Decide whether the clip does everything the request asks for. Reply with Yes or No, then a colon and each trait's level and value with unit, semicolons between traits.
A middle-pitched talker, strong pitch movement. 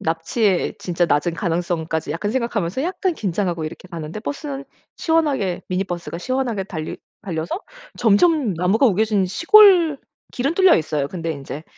No: high, 195 Hz; wide, 8.0 semitones